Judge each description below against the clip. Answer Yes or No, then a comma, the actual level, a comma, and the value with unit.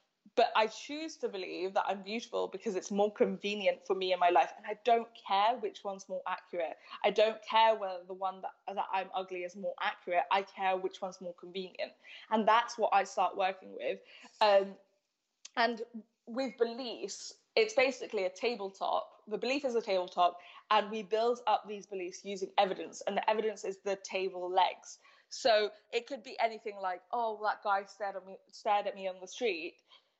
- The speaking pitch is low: No, high, 205 Hz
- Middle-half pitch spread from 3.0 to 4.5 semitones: Yes, average, 3.5 semitones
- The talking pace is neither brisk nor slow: No, fast, 210 wpm